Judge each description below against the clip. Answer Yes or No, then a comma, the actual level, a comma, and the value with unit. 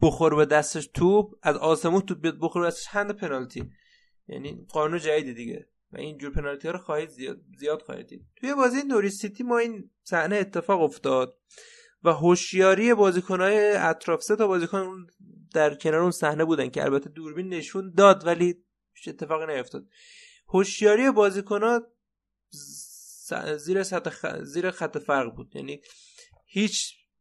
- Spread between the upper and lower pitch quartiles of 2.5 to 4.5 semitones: No, average, 4.9 semitones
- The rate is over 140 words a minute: Yes, average, 150 wpm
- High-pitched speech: No, medium, 180 Hz